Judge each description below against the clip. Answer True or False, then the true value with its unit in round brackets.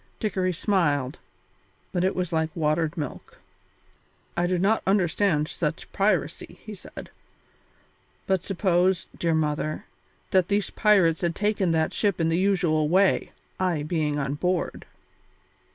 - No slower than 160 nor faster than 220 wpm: False (135 wpm)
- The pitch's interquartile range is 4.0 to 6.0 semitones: False (3.3 semitones)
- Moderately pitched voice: True (175 Hz)